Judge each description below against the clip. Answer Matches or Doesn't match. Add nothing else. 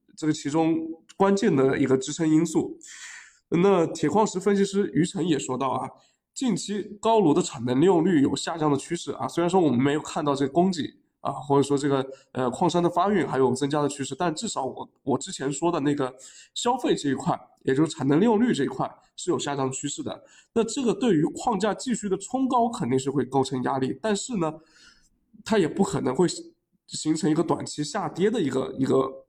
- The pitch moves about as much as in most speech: Doesn't match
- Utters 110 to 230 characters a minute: Doesn't match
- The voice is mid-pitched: Matches